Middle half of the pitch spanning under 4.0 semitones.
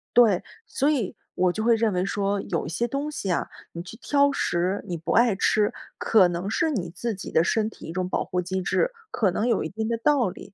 No: average, 4.5 semitones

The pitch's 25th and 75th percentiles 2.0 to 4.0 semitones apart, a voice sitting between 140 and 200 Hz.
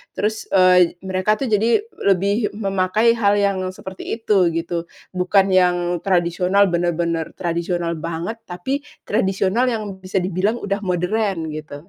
Yes: average, 2.8 semitones; medium, 185 Hz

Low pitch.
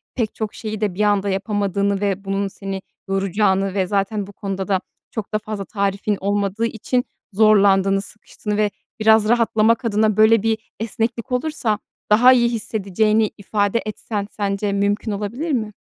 No: high, 210 Hz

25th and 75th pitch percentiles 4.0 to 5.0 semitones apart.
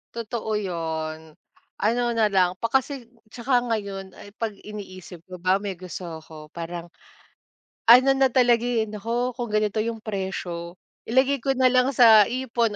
Yes: average, 4.7 semitones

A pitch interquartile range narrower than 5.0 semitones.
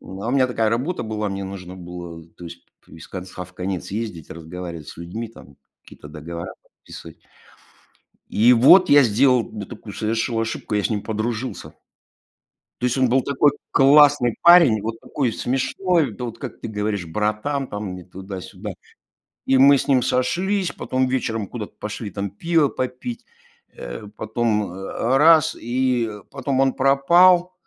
No: wide, 5.4 semitones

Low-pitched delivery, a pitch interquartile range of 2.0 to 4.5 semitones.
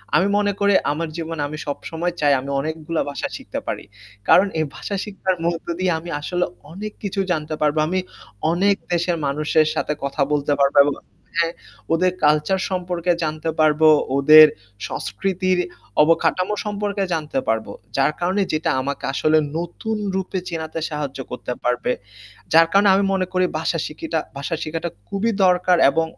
No: medium, 165 Hz; average, 3.3 semitones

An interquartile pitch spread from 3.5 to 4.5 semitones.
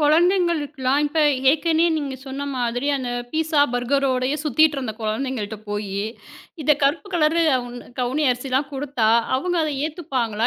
Yes: average, 3.8 semitones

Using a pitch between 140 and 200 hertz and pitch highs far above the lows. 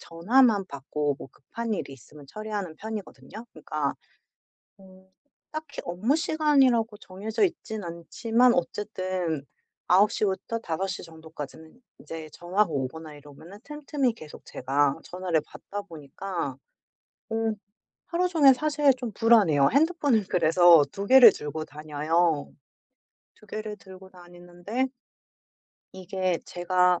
Yes: medium, 185 Hz; wide, 6.0 semitones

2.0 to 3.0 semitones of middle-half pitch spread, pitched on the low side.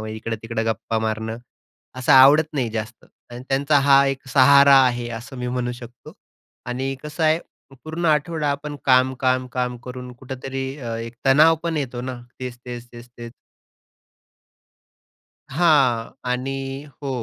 Yes: narrow, 2.5 semitones; low, 130 Hz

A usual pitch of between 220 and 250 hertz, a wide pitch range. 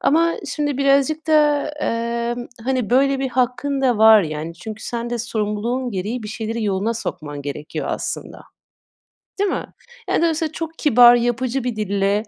No: high, 240 Hz; average, 4.3 semitones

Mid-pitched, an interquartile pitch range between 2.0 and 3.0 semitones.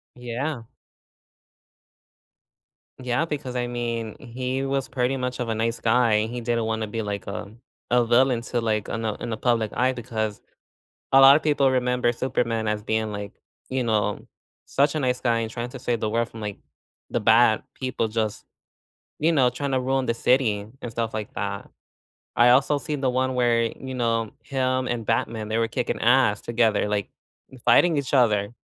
No: low, 120 Hz; narrow, 2.6 semitones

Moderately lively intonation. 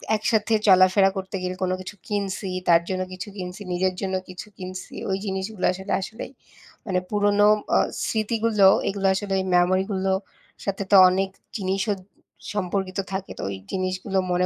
No: narrow, 1.6 semitones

